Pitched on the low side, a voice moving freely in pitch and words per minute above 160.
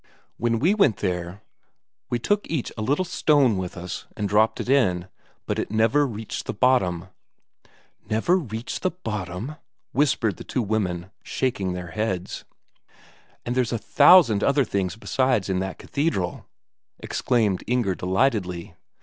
No: low, 110 Hz; wide, 5.8 semitones; average, 145 wpm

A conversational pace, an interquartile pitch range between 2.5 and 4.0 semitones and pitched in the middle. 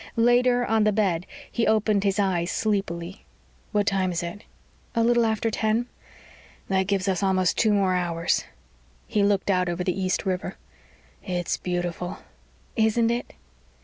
No: average, 150 wpm; average, 3.3 semitones; high, 195 Hz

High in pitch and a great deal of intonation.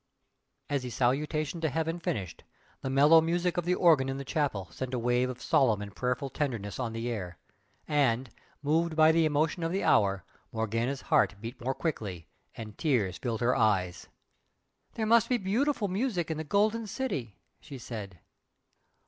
No: low, 135 Hz; wide, 6.2 semitones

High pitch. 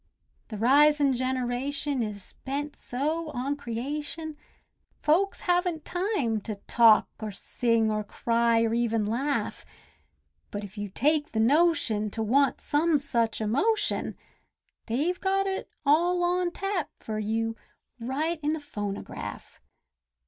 Yes: very high, 270 Hz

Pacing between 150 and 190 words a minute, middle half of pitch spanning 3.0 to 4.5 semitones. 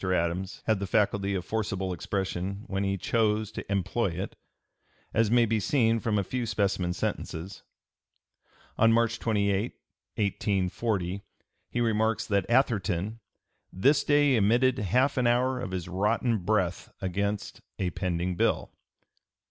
No: slow, 135 wpm; average, 3.4 semitones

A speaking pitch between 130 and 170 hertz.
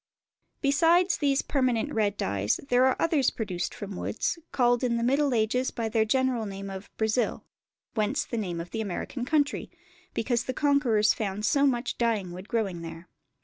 No: high, 235 Hz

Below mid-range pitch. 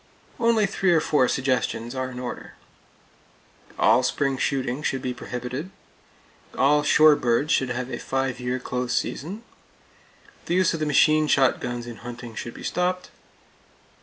Yes: low, 130 Hz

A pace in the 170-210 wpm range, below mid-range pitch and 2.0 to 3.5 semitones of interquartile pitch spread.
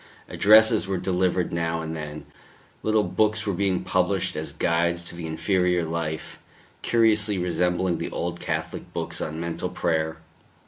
No: average, 145 wpm; very low, 90 Hz; average, 2.9 semitones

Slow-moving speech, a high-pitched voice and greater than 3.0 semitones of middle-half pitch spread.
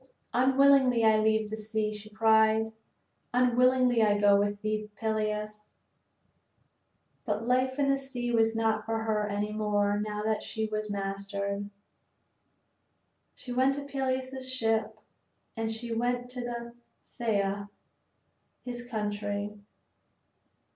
No: slow, 120 wpm; high, 220 Hz; average, 2.7 semitones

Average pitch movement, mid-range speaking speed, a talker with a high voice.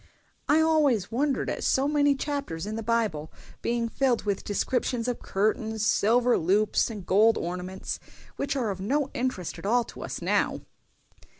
Yes: average, 4.7 semitones; average, 165 wpm; high, 230 Hz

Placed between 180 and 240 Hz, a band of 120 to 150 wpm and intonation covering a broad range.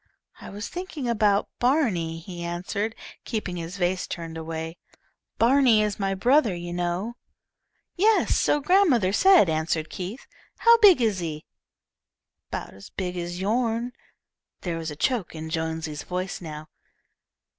Yes: high, 190 Hz; average, 140 wpm; wide, 6.2 semitones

